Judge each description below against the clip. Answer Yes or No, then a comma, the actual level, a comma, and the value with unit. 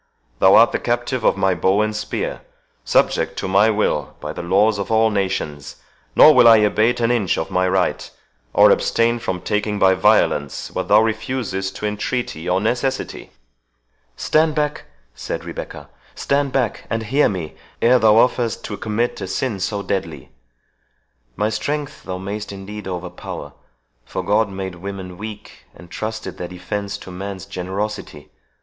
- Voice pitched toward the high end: No, low, 105 Hz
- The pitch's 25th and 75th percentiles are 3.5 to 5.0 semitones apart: No, average, 3.1 semitones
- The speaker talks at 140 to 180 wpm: Yes, average, 155 wpm